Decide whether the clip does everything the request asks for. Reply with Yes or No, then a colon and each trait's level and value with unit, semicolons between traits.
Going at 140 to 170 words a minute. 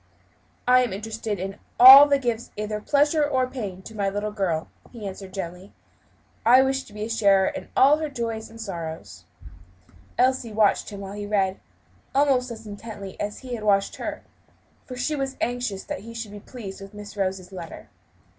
No: average, 185 wpm